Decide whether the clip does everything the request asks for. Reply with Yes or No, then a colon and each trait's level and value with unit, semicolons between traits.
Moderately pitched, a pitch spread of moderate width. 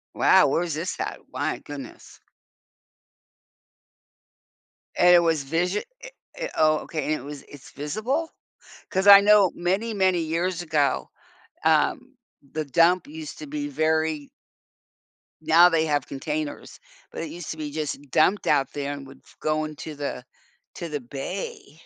Yes: medium, 160 Hz; average, 3.7 semitones